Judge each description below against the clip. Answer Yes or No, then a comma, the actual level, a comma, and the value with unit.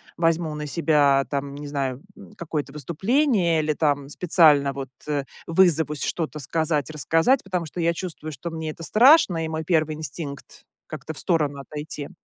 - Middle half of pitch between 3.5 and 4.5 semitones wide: No, average, 2.7 semitones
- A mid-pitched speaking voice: Yes, medium, 155 Hz